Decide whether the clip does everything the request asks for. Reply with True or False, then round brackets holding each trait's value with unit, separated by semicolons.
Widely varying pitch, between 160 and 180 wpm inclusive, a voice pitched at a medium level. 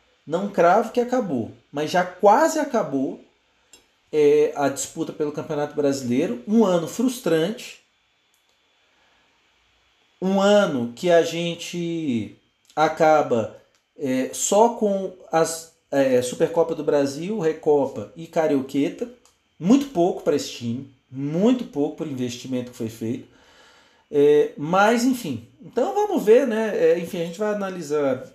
False (7.2 semitones; 125 wpm; 170 Hz)